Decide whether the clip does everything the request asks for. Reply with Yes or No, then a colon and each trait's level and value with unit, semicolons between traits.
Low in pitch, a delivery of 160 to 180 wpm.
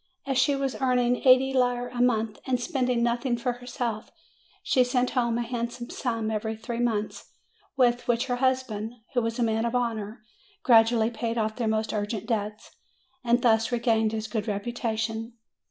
No: high, 235 Hz; average, 170 wpm